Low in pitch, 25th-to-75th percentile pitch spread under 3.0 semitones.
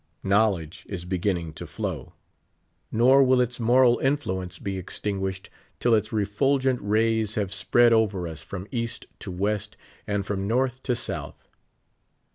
No: low, 105 Hz; average, 3.8 semitones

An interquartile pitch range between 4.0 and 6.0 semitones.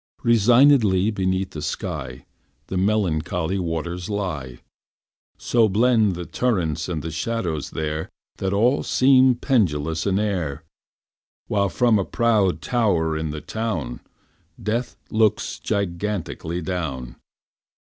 Yes: wide, 5.4 semitones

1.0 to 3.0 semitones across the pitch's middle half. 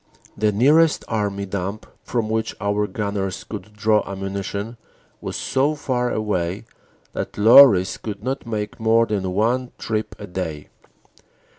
Yes: narrow, 2.6 semitones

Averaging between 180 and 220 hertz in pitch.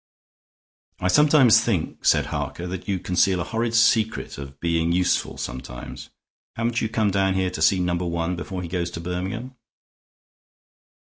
No: very low, 90 Hz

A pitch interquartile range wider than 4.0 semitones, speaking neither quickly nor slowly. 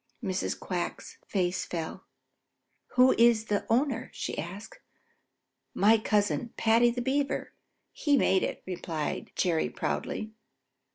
No: average, 4.5 semitones; slow, 115 wpm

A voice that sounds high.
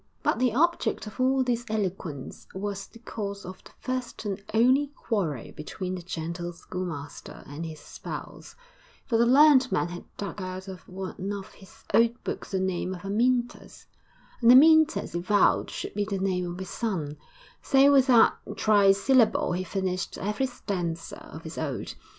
Yes: high, 200 Hz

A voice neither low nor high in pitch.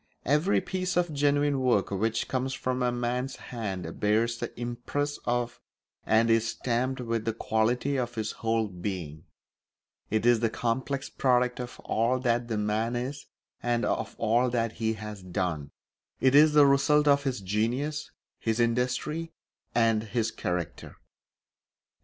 No: low, 120 Hz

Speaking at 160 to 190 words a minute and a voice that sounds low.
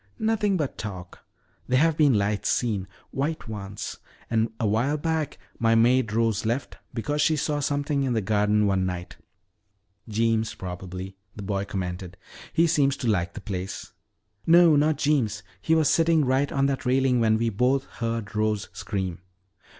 Yes: average, 165 wpm; low, 115 Hz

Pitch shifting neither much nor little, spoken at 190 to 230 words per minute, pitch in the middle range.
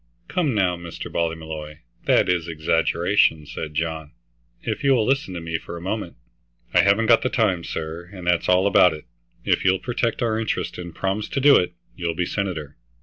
No: average, 4.5 semitones; average, 195 wpm; very low, 90 Hz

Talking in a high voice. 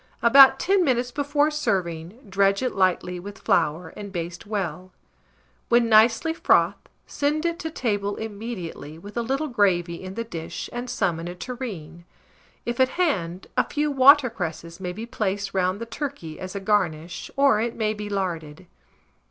Yes: high, 205 Hz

